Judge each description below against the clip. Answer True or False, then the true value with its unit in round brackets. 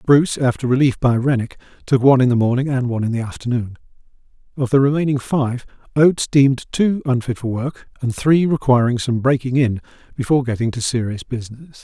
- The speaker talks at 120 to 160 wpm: False (180 wpm)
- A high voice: False (130 Hz)